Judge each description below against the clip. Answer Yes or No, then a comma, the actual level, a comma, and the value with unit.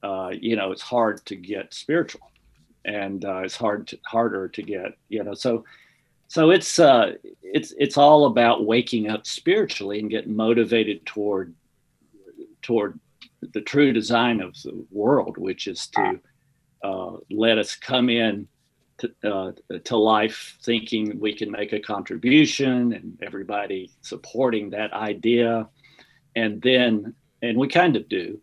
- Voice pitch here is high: No, low, 115 Hz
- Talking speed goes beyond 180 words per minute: No, average, 150 wpm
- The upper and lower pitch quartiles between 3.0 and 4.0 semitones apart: Yes, average, 3.7 semitones